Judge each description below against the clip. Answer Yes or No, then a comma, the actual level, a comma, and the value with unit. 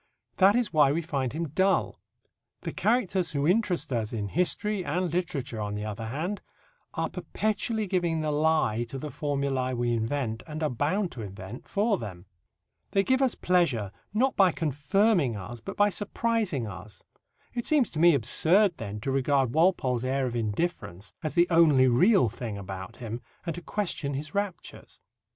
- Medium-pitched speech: Yes, medium, 150 Hz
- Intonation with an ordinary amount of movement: No, wide, 7.6 semitones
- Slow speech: No, average, 175 wpm